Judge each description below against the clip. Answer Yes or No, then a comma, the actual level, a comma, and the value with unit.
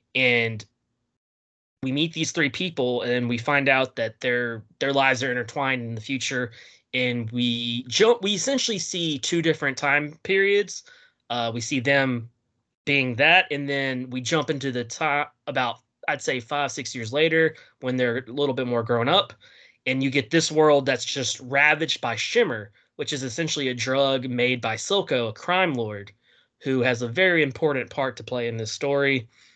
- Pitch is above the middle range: No, low, 135 Hz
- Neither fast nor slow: Yes, average, 180 wpm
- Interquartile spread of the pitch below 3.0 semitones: No, average, 3.6 semitones